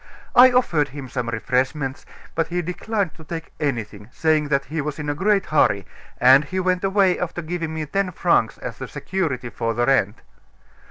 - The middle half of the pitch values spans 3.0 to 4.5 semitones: No, wide, 5.5 semitones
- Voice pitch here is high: No, medium, 155 Hz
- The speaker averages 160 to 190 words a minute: Yes, average, 180 wpm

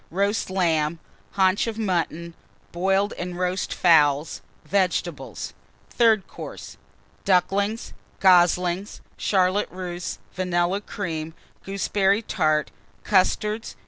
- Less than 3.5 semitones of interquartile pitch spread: Yes, narrow, 2.4 semitones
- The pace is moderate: No, slow, 90 wpm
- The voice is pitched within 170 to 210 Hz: Yes, medium, 185 Hz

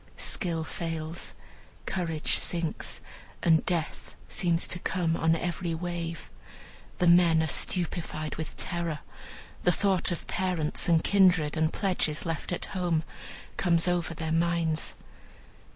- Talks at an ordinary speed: No, slow, 125 wpm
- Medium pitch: Yes, medium, 170 Hz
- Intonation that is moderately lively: No, narrow, 1.6 semitones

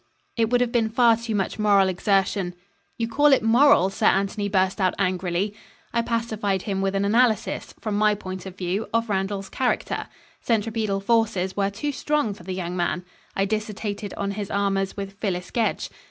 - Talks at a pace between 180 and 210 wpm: Yes, average, 185 wpm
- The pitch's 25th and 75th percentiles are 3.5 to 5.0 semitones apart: No, average, 2.7 semitones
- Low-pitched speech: No, high, 200 Hz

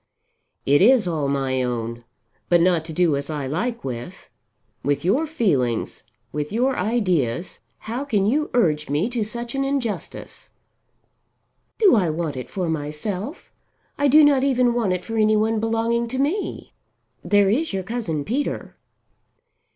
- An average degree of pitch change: No, wide, 8.1 semitones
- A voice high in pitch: Yes, high, 205 Hz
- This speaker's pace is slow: No, average, 155 wpm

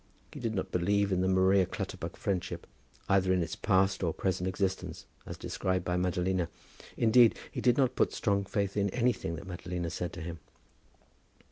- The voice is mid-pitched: No, very low, 95 Hz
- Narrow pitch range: Yes, narrow, 2.0 semitones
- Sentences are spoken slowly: No, average, 175 wpm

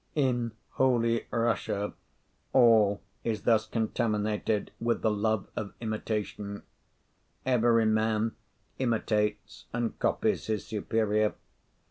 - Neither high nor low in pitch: No, low, 110 Hz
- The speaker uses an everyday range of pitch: No, narrow, 1.6 semitones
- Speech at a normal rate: No, slow, 95 wpm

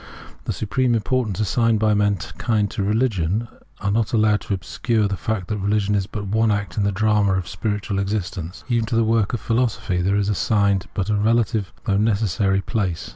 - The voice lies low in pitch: Yes, low, 105 Hz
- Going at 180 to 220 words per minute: Yes, average, 190 wpm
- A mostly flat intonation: Yes, narrow, 2.1 semitones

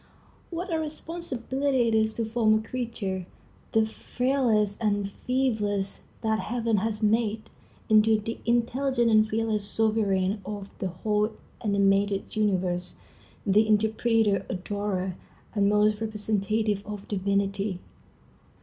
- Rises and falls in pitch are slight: Yes, narrow, 2.1 semitones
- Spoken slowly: Yes, slow, 115 wpm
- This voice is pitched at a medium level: No, high, 215 Hz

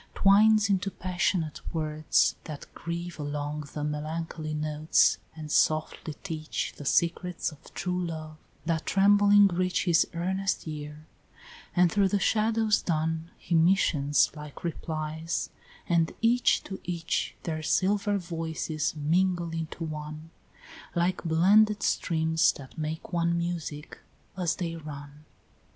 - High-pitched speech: No, medium, 165 Hz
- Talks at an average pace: No, slow, 125 wpm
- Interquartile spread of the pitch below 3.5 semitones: Yes, average, 2.9 semitones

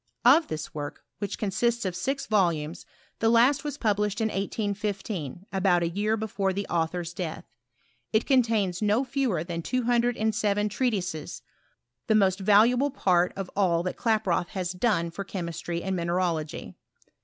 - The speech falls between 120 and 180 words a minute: Yes, average, 160 wpm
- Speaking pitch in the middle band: No, high, 200 Hz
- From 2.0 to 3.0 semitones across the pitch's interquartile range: No, average, 4.2 semitones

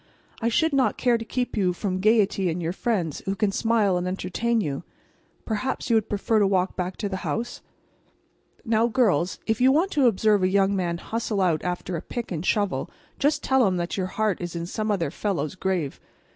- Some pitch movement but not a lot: Yes, average, 4.0 semitones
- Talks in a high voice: Yes, high, 200 Hz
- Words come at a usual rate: No, fast, 210 wpm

